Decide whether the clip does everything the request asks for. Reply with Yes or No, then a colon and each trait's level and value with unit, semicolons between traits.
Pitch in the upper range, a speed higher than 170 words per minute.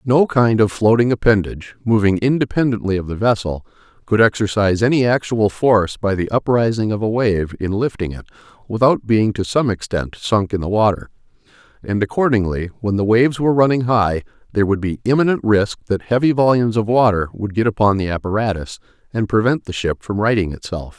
No: low, 110 Hz; average, 180 wpm